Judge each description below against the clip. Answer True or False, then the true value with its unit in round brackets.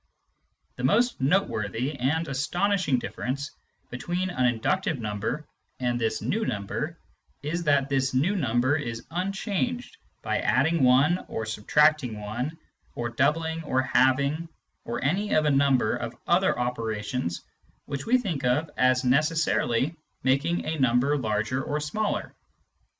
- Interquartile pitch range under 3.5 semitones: False (4.9 semitones)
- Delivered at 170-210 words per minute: False (135 wpm)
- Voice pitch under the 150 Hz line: True (140 Hz)